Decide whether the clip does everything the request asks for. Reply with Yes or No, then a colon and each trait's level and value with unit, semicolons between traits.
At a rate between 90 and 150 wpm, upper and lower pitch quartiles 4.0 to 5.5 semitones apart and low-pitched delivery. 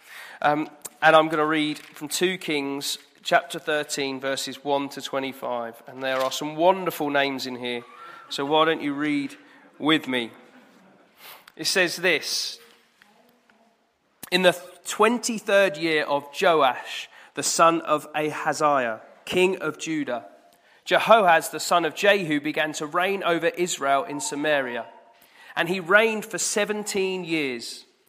No: slow, 135 wpm; average, 4.7 semitones; medium, 160 Hz